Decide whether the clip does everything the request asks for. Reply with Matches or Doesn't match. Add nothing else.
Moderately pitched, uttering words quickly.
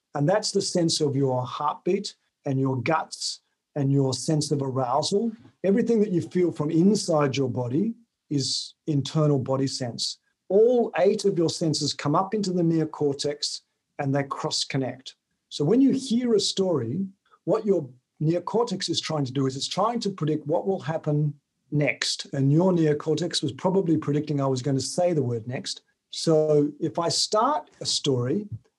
Doesn't match